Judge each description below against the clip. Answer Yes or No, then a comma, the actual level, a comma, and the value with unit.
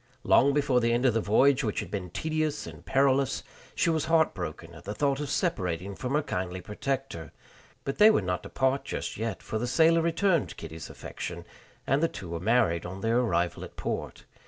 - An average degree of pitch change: No, wide, 7.7 semitones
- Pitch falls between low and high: No, low, 125 Hz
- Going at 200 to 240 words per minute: Yes, fast, 205 wpm